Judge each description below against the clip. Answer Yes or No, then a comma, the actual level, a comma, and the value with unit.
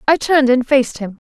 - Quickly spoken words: Yes, fast, 235 wpm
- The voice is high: Yes, very high, 260 Hz